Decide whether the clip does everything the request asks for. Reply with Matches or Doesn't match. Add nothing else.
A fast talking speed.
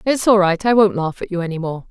Matches